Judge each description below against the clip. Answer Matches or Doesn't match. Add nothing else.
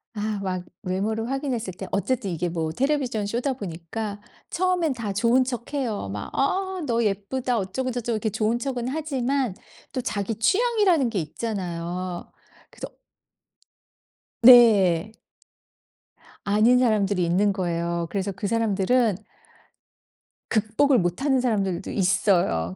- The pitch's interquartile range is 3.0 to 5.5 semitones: Matches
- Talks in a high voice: Matches